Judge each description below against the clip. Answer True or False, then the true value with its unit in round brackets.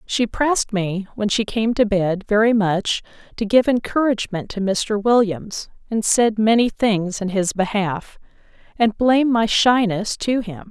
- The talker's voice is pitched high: True (215 Hz)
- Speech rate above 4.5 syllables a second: False (4.3 syllables/s)